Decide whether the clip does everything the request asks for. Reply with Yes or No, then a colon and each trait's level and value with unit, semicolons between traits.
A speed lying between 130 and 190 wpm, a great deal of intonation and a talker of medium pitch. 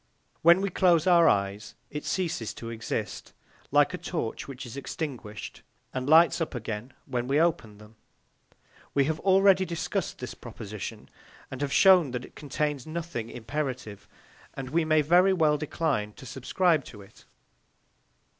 Yes: average, 155 wpm; wide, 5.8 semitones; medium, 145 Hz